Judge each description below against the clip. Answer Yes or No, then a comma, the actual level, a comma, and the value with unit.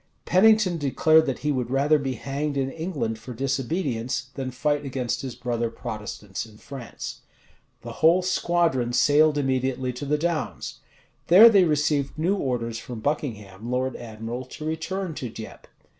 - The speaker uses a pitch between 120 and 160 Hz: Yes, low, 135 Hz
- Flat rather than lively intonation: No, average, 4.3 semitones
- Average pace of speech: Yes, average, 155 wpm